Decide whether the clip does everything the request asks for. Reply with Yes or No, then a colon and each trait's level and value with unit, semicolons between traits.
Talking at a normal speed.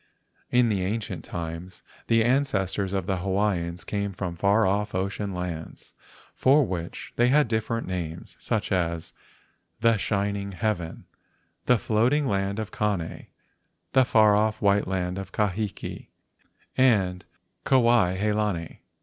No: slow, 130 wpm